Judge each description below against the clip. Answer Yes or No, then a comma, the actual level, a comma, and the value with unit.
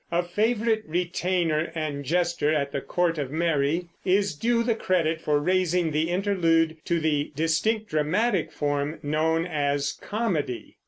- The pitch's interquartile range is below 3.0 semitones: No, average, 3.4 semitones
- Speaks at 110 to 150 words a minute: Yes, average, 145 wpm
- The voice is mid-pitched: Yes, medium, 165 Hz